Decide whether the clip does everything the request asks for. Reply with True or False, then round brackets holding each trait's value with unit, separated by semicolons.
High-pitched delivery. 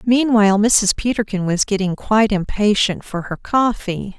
True (210 Hz)